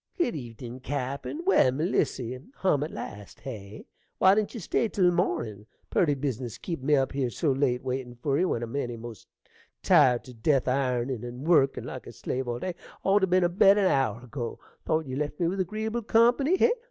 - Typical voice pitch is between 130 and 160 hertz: Yes, medium, 140 Hz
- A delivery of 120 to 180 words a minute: No, average, 200 wpm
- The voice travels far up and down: Yes, wide, 6.8 semitones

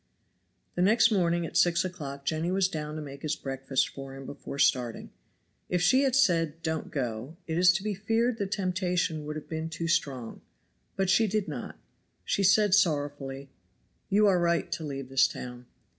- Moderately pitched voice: Yes, medium, 165 Hz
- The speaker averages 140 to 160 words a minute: No, average, 185 wpm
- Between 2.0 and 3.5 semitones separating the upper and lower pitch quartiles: No, average, 5.2 semitones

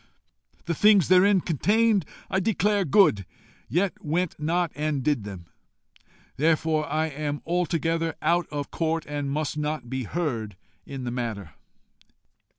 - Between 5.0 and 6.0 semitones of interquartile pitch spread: No, average, 3.8 semitones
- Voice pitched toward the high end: No, medium, 155 Hz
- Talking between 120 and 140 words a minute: Yes, slow, 135 wpm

